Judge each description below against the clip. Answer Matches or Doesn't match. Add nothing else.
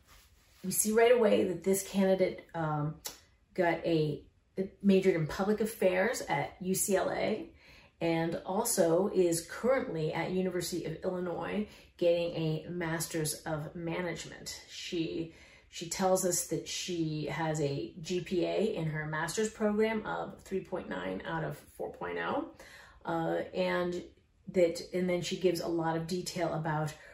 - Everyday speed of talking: Doesn't match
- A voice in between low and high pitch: Matches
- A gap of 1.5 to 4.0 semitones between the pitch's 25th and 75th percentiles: Matches